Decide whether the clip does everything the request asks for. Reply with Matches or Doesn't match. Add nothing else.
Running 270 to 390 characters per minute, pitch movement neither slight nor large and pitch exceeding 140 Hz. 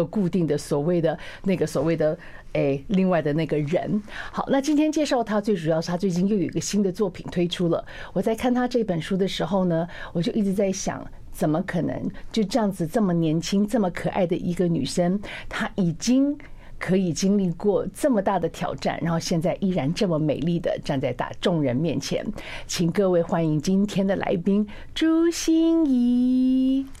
Matches